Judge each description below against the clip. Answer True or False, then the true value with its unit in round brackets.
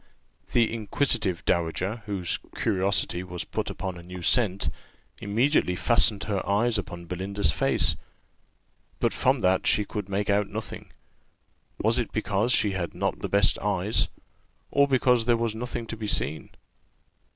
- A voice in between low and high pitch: False (100 Hz)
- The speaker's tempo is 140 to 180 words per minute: True (150 wpm)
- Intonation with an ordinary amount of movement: True (3.7 semitones)